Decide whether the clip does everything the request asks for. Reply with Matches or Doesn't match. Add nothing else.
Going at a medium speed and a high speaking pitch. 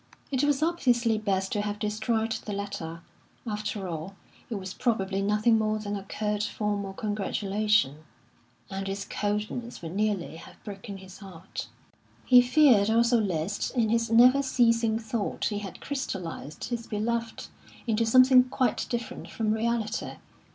Matches